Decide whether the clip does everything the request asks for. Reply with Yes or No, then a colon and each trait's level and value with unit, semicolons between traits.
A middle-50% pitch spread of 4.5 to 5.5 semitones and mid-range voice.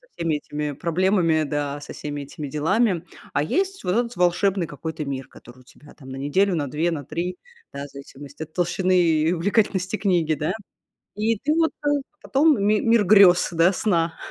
Yes: average, 5.0 semitones; medium, 170 Hz